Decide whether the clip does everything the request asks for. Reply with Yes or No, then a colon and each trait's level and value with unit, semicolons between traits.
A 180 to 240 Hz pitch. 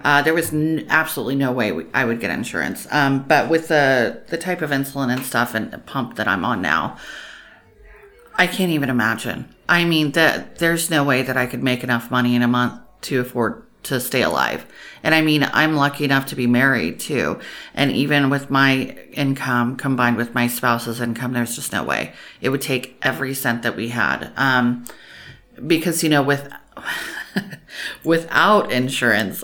No: low, 135 Hz